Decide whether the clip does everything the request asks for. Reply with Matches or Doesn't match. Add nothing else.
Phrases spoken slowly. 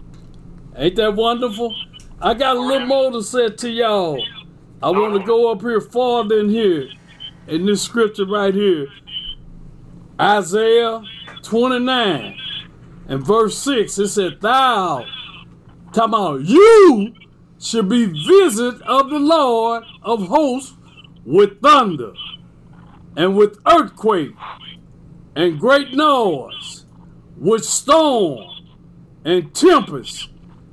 Matches